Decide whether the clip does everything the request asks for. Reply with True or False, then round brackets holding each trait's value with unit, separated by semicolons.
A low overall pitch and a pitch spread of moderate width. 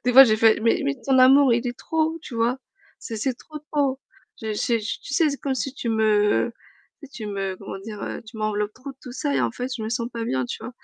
False (235 Hz; 3.6 semitones)